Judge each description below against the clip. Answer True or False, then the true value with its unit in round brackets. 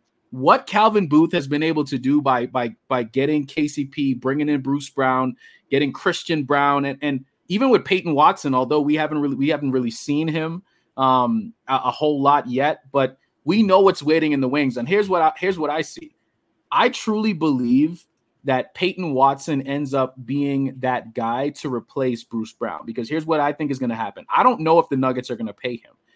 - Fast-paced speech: True (210 wpm)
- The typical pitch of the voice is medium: True (145 Hz)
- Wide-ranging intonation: False (3.3 semitones)